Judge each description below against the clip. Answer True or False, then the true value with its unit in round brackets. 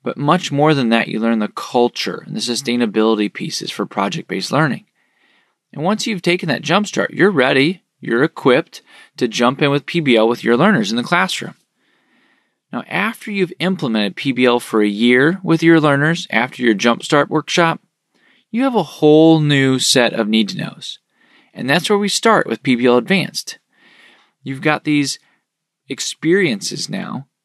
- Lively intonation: True (7.0 semitones)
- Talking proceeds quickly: False (170 wpm)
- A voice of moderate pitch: True (145 Hz)